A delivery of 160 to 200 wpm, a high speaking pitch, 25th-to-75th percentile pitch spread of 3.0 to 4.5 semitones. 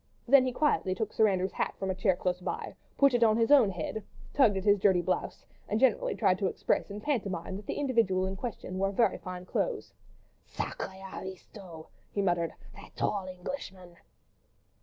Yes: average, 185 wpm; high, 195 Hz; average, 3.9 semitones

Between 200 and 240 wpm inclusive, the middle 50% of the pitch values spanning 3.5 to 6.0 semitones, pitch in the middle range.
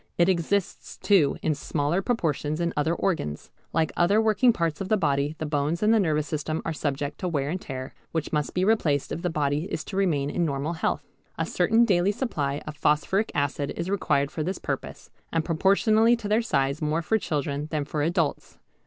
Yes: fast, 205 wpm; average, 4.7 semitones; medium, 160 Hz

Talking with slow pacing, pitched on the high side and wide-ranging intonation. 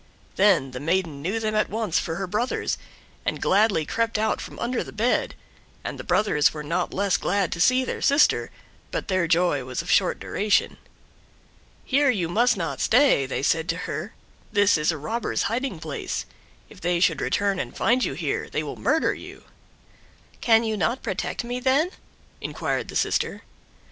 No: average, 180 wpm; high, 200 Hz; wide, 5.9 semitones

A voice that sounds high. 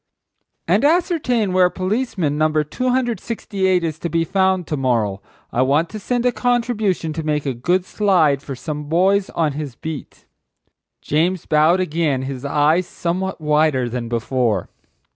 No: medium, 165 Hz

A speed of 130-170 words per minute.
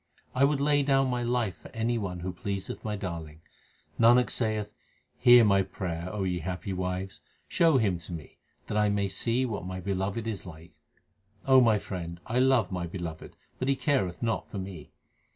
No: average, 190 wpm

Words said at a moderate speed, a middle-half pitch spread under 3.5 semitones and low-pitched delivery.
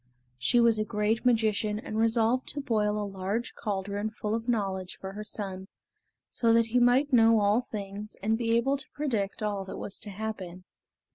No: average, 190 wpm; narrow, 2.4 semitones; high, 215 Hz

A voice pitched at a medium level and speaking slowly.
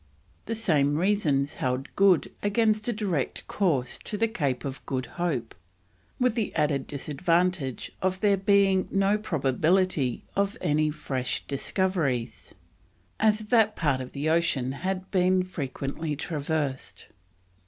Yes: medium, 170 Hz; slow, 130 wpm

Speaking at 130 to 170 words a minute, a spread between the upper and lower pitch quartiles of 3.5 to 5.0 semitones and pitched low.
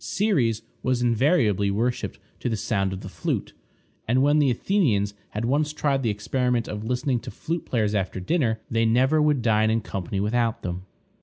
No: average, 180 wpm; average, 4.2 semitones; low, 115 Hz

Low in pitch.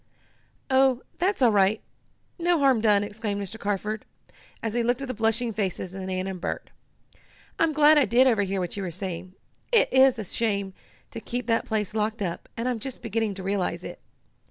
No: high, 220 Hz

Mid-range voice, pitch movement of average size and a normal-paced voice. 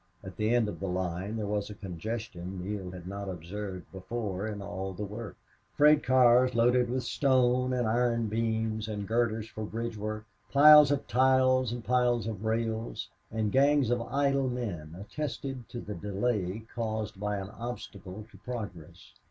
No: low, 110 Hz; average, 3.5 semitones; average, 170 wpm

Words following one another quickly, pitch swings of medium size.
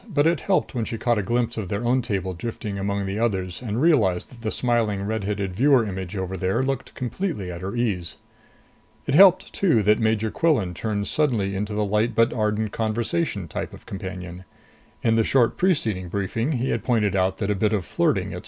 Yes: fast, 210 wpm; average, 3.6 semitones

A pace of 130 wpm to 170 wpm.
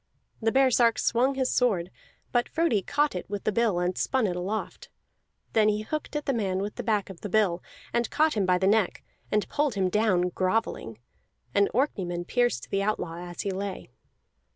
No: average, 195 wpm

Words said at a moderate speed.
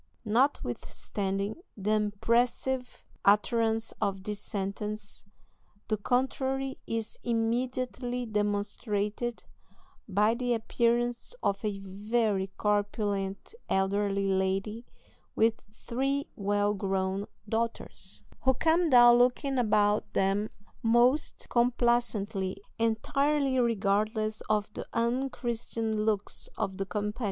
No: slow, 95 wpm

